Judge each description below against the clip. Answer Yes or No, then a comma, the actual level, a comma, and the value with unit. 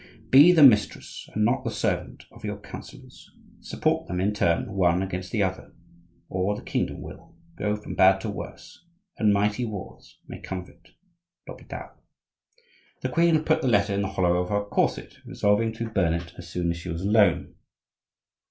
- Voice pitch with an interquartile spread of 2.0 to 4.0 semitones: Yes, average, 3.0 semitones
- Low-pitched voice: Yes, low, 100 Hz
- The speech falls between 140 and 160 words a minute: No, average, 180 wpm